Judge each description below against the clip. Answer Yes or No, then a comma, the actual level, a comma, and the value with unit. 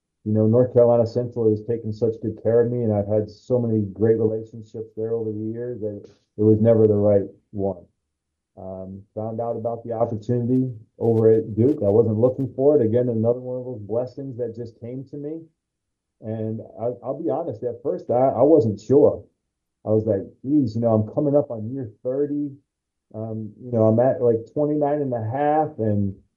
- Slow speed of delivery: No, fast, 205 wpm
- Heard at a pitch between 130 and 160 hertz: No, low, 115 Hz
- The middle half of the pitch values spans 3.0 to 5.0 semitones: No, narrow, 2.5 semitones